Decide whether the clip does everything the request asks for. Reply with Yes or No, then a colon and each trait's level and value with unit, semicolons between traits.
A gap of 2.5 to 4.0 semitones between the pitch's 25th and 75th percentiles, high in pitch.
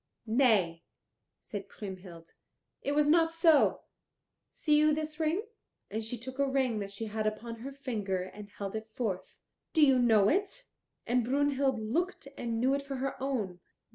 No: average, 5.1 semitones; high, 245 Hz